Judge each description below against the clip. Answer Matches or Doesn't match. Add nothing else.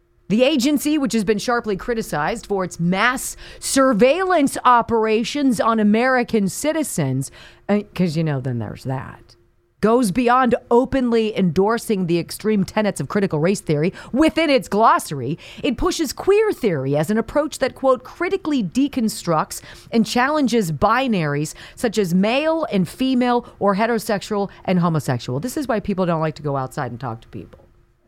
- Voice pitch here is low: Doesn't match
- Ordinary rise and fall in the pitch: Doesn't match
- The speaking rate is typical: Matches